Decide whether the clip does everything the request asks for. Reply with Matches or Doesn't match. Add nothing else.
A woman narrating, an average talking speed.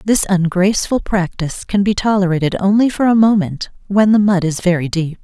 Matches